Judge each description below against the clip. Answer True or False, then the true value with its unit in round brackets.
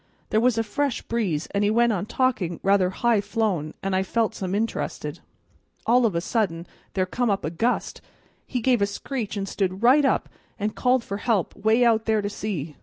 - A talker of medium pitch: False (215 Hz)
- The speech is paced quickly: True (210 wpm)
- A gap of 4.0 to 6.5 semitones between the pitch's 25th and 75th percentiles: False (3.6 semitones)